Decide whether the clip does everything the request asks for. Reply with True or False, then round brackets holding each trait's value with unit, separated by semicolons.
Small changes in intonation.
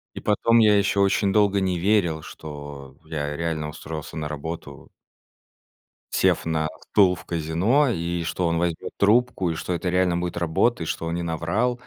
False (3.8 semitones)